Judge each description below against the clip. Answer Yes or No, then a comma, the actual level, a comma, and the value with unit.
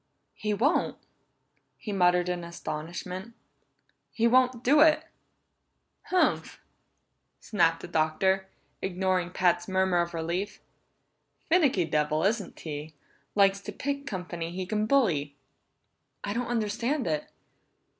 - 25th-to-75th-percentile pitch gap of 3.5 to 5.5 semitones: Yes, average, 5.2 semitones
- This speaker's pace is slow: Yes, slow, 110 wpm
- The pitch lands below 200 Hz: Yes, high, 190 Hz